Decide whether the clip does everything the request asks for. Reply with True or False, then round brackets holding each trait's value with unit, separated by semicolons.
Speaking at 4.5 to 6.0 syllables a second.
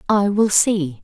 False (3.5 syllables/s)